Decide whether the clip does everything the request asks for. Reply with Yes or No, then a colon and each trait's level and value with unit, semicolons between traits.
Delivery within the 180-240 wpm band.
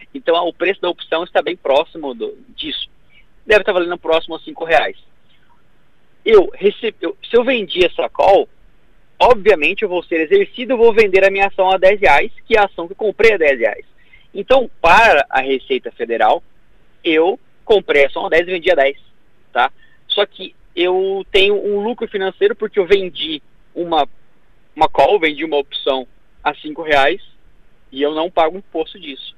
Yes: fast, 185 wpm